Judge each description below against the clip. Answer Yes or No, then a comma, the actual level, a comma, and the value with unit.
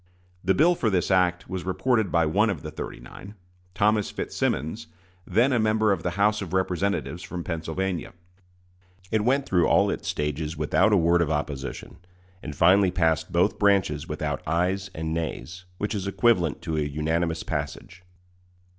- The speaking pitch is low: Yes, very low, 90 Hz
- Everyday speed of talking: Yes, average, 165 wpm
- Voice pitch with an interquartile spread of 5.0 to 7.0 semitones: No, average, 3.9 semitones